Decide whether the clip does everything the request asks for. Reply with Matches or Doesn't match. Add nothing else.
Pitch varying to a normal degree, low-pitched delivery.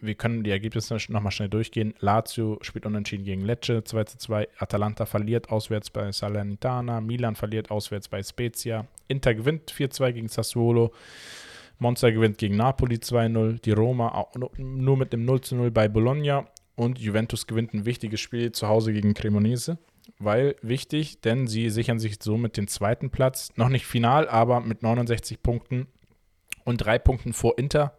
Doesn't match